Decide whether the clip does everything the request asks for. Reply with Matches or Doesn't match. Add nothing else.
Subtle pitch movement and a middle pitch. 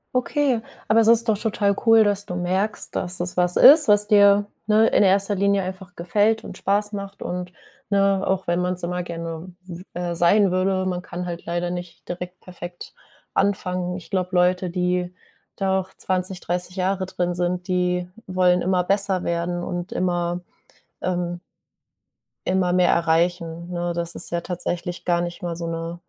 Matches